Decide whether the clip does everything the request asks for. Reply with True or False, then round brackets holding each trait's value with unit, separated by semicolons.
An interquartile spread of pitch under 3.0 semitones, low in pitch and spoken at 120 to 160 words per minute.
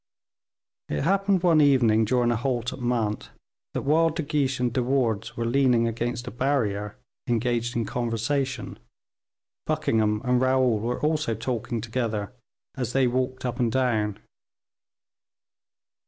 True (2.5 semitones; 125 Hz; 140 wpm)